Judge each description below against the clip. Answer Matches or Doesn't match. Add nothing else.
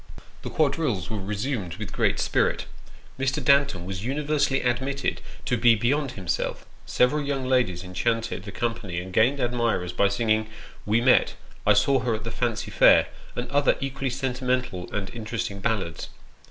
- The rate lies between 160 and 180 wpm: Matches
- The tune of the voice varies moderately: Matches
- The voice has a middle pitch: Doesn't match